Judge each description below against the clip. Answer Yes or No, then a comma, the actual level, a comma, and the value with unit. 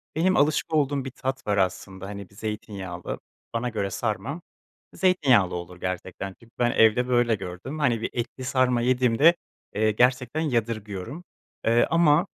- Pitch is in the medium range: No, low, 120 Hz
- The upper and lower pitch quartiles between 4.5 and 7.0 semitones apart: Yes, average, 5.0 semitones